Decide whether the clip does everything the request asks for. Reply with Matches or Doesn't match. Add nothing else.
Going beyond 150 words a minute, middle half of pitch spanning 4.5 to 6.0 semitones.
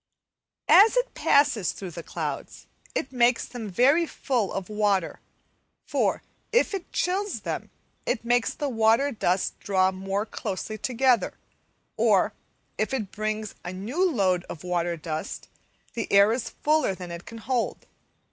Doesn't match